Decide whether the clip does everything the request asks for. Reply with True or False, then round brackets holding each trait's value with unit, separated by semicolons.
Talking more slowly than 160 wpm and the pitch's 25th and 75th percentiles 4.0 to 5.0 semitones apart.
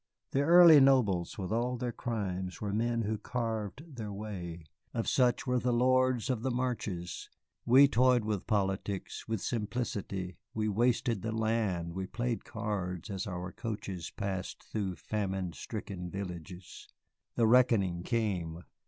True (145 wpm; 4.4 semitones)